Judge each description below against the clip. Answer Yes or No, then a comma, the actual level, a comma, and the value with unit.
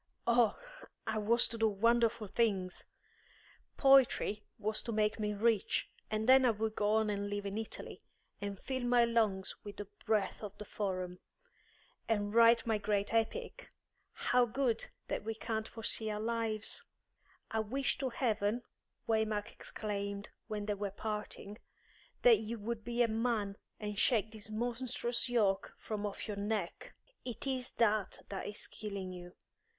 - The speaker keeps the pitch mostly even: Yes, narrow, 2.1 semitones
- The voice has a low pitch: No, high, 215 Hz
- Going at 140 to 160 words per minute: Yes, average, 155 wpm